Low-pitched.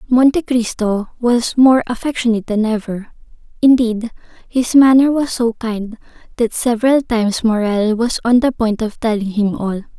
No: high, 230 Hz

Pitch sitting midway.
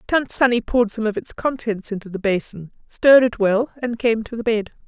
No: high, 225 Hz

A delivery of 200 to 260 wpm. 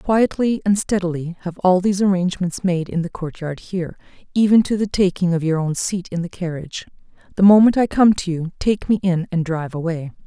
Yes: fast, 205 wpm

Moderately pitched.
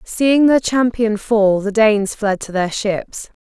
No: high, 215 Hz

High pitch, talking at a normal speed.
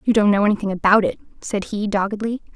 No: high, 210 Hz; fast, 210 wpm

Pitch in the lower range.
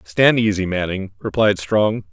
Yes: low, 105 Hz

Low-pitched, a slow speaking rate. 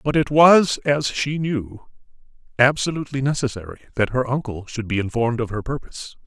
No: low, 130 Hz; average, 165 wpm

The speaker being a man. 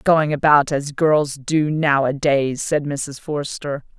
No: female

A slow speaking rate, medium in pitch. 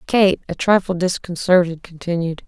Yes: slow, 120 wpm; medium, 175 Hz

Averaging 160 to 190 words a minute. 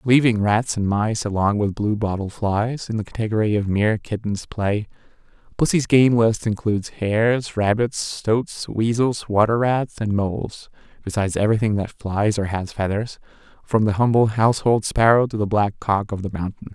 Yes: average, 170 wpm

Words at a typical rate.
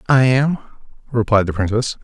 Yes: average, 145 wpm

